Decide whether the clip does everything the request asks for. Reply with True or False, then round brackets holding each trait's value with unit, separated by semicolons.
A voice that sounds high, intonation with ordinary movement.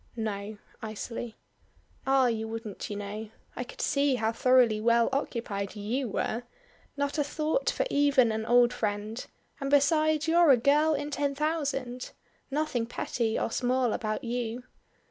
True (245 Hz; 4.3 semitones)